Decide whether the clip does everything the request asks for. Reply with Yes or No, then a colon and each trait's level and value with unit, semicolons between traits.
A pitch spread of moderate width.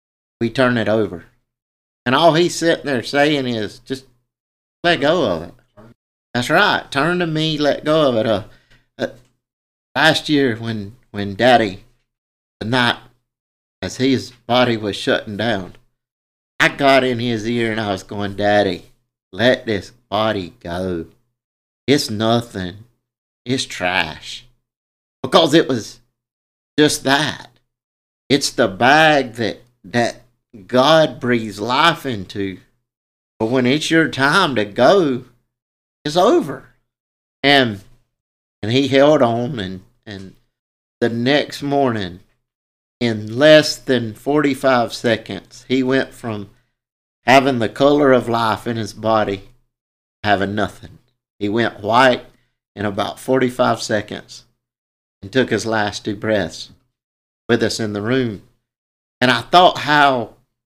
Yes: average, 3.8 semitones